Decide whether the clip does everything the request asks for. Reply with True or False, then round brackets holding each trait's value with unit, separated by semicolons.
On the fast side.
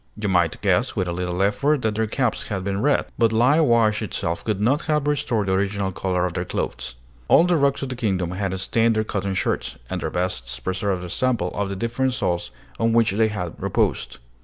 True (220 wpm)